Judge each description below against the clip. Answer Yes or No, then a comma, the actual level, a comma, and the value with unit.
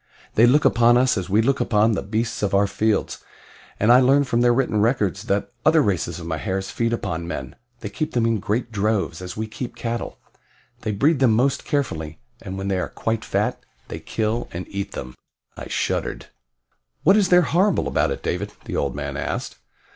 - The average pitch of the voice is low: Yes, low, 110 Hz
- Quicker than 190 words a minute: Yes, average, 200 wpm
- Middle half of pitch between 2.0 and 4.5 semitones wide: Yes, average, 4.1 semitones